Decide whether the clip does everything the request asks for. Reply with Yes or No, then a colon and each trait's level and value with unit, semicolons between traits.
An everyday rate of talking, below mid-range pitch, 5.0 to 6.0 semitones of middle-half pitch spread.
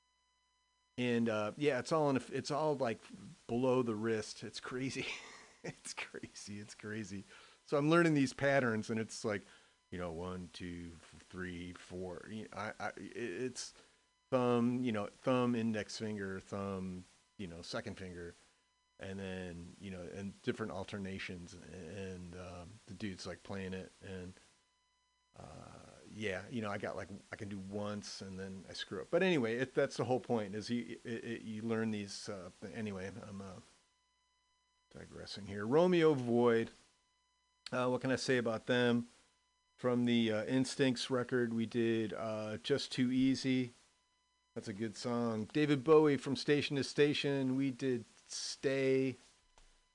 Yes: average, 160 wpm; low, 120 Hz; wide, 5.5 semitones